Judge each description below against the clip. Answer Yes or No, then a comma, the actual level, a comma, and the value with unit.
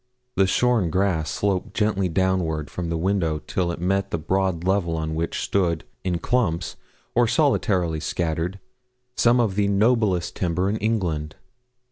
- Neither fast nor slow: Yes, average, 150 wpm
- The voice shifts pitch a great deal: No, average, 3.3 semitones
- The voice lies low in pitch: Yes, very low, 95 Hz